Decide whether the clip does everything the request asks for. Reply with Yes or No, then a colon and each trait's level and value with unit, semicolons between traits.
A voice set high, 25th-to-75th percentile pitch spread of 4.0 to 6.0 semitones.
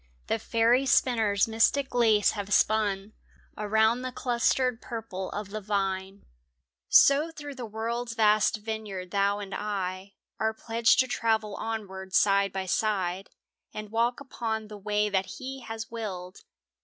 No: high, 215 Hz; average, 2.7 semitones